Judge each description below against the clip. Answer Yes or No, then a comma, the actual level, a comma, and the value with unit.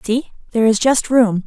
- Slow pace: No, fast, 205 wpm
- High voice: Yes, high, 230 Hz